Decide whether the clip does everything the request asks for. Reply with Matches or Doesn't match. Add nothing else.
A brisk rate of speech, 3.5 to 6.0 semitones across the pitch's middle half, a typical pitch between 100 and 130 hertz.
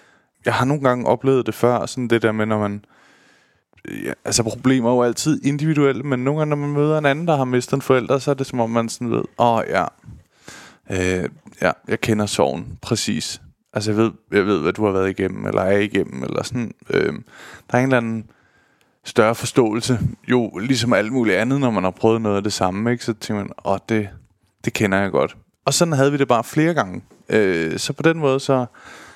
Matches